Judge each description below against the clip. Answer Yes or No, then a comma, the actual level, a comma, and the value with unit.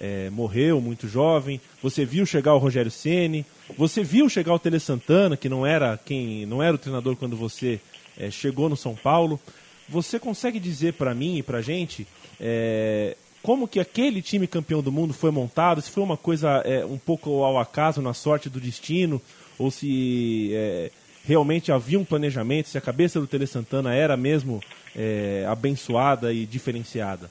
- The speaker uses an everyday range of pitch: Yes, average, 4.9 semitones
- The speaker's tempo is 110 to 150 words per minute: No, average, 180 wpm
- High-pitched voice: No, medium, 140 Hz